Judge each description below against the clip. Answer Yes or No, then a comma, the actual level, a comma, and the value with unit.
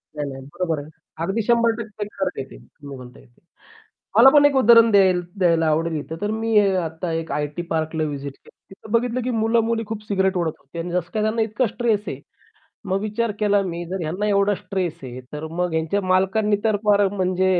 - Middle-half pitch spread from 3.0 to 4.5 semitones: No, average, 5.2 semitones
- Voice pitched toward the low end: No, high, 190 Hz